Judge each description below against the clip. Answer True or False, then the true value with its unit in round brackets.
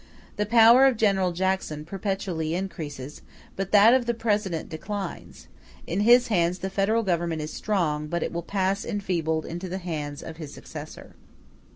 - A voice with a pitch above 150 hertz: True (190 Hz)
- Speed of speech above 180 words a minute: False (165 wpm)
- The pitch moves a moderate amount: True (4.1 semitones)